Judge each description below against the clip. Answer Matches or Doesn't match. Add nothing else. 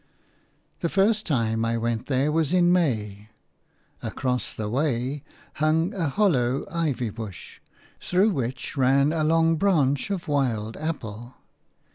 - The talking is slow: Matches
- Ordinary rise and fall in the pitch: Doesn't match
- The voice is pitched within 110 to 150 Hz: Matches